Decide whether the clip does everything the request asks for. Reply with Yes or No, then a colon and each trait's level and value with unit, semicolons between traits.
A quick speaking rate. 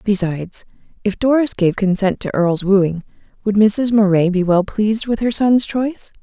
No: average, 175 wpm